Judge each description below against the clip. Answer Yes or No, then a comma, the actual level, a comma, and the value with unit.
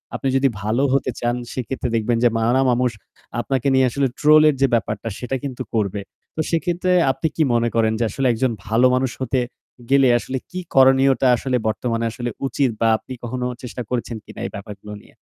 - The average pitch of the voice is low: Yes, low, 125 Hz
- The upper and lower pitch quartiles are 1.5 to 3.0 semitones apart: Yes, narrow, 2.5 semitones